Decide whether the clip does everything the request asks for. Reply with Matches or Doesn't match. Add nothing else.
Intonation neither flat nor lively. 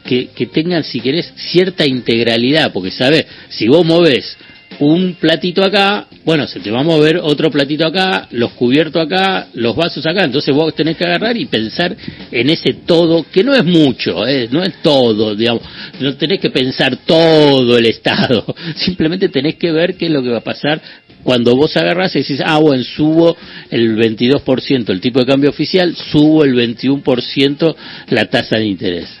Matches